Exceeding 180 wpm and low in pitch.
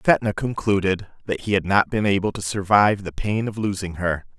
Yes: fast, 205 wpm; low, 100 Hz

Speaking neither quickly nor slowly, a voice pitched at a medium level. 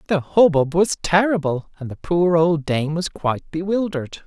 Yes: average, 170 wpm; medium, 165 Hz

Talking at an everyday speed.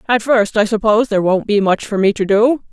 No: fast, 265 wpm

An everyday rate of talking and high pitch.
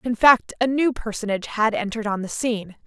No: fast, 210 wpm; high, 225 Hz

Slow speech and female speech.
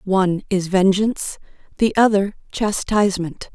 Yes: slow, 100 wpm; female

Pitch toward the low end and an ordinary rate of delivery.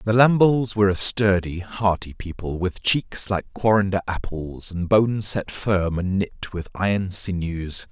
Yes: very low, 95 Hz; average, 160 wpm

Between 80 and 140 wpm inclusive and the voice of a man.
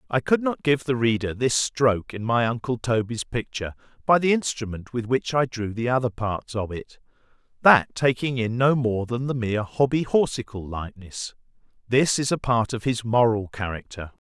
No: average, 175 wpm; male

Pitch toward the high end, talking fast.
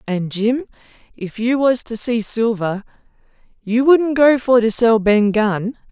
No: high, 230 Hz; average, 160 wpm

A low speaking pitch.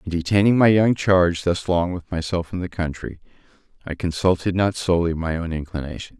Yes: very low, 90 Hz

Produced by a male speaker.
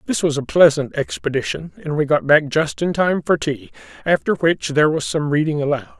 Yes: male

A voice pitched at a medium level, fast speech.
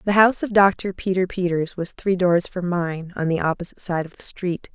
Yes: medium, 180 Hz; fast, 230 wpm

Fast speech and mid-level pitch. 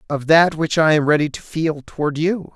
Yes: fast, 235 wpm; medium, 155 Hz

